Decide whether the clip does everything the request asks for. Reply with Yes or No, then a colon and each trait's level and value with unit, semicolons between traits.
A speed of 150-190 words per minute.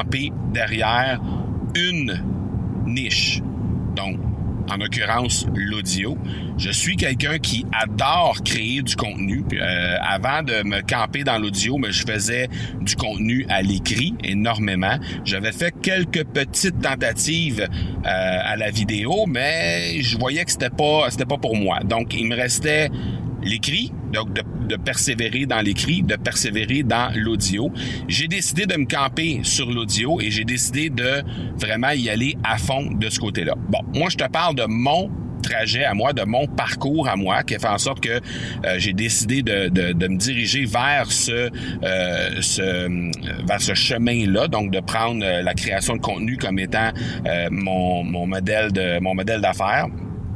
Yes: average, 165 wpm